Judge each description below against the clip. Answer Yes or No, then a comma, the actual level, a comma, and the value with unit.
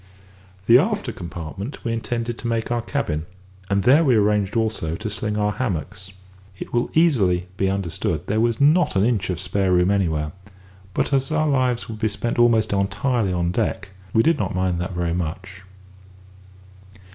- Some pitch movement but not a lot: Yes, average, 4.5 semitones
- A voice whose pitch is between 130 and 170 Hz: No, low, 105 Hz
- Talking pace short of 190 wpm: Yes, average, 180 wpm